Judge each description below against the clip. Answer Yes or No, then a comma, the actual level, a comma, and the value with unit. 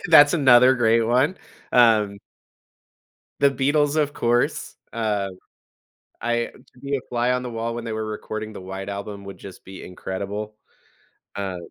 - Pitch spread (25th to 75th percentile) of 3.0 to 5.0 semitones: Yes, average, 3.9 semitones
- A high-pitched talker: No, low, 115 Hz